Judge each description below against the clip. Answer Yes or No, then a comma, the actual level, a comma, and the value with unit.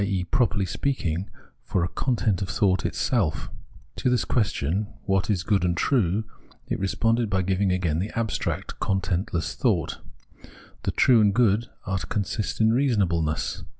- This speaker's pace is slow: No, average, 150 wpm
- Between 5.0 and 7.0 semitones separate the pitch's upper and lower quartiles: No, average, 3.5 semitones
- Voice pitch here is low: Yes, low, 100 Hz